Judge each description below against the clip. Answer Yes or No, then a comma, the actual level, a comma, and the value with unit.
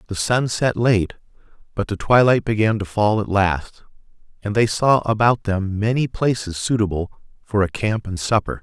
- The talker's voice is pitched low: Yes, low, 105 Hz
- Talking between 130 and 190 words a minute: Yes, average, 175 wpm